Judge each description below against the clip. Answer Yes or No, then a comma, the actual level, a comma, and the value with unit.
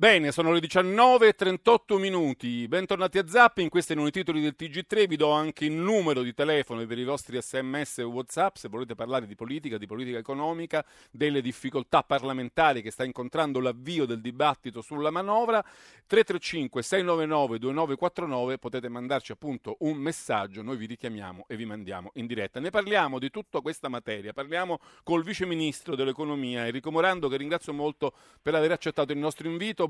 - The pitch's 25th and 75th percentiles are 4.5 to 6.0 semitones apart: Yes, average, 5.3 semitones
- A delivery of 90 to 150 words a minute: No, average, 165 wpm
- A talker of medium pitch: Yes, medium, 150 Hz